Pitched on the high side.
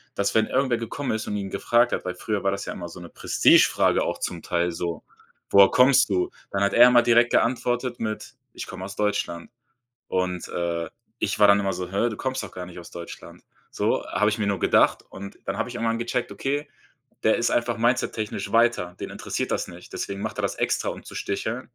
No: low, 105 Hz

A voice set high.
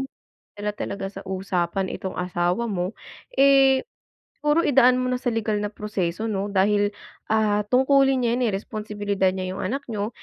Yes: high, 210 Hz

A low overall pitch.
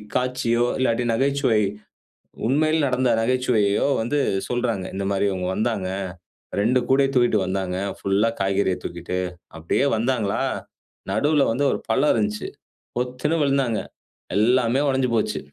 Yes: low, 120 Hz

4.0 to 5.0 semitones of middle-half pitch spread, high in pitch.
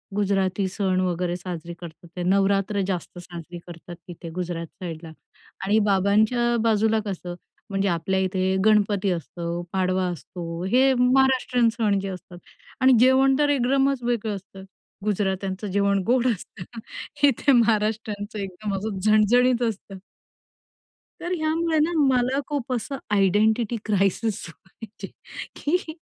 Yes: average, 4.5 semitones; high, 205 Hz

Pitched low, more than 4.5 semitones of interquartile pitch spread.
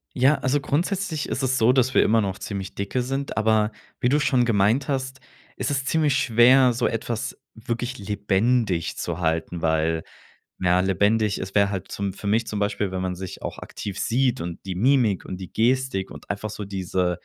Yes: low, 110 Hz; average, 5.3 semitones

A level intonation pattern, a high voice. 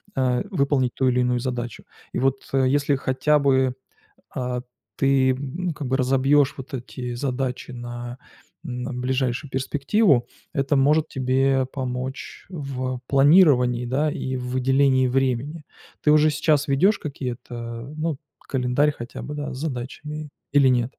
No: narrow, 2.2 semitones; low, 130 Hz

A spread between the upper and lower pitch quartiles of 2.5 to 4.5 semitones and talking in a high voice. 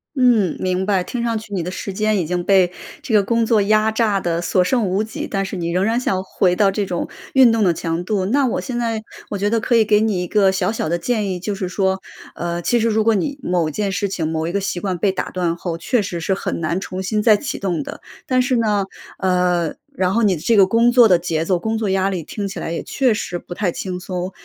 Yes: average, 3.4 semitones; high, 195 Hz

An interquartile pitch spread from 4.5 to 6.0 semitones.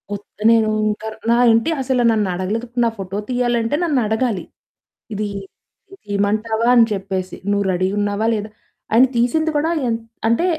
No: average, 2.9 semitones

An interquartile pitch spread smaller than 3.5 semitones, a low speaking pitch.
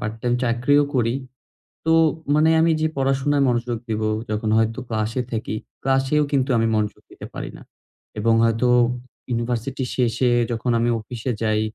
Yes: average, 3.0 semitones; low, 120 Hz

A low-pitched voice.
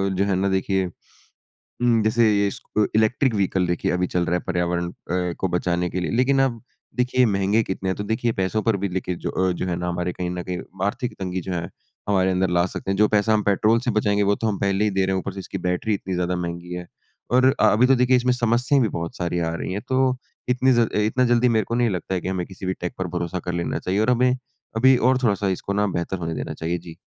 Yes: very low, 95 Hz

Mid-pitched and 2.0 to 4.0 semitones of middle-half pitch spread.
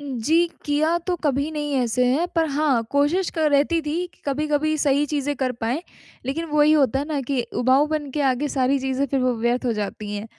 No: very high, 285 Hz; average, 2.9 semitones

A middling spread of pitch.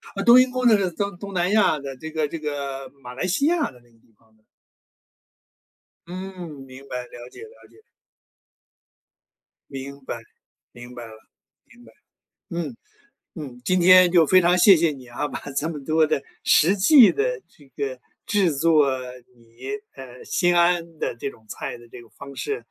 No: wide, 5.9 semitones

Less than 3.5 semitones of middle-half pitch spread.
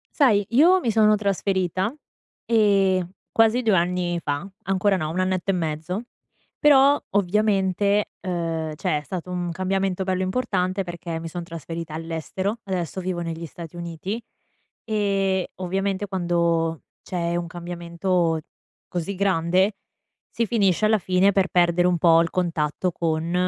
Yes: average, 2.7 semitones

